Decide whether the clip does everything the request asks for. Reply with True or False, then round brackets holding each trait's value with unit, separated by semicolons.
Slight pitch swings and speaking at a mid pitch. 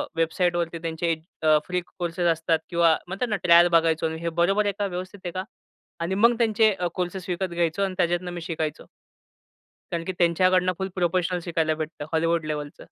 True (2.0 semitones; 175 Hz)